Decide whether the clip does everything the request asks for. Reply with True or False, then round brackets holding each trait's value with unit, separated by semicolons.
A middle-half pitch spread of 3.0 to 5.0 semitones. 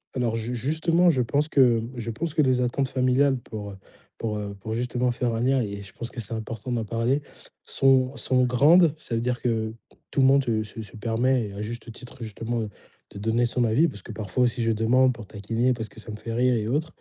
False (2.6 semitones)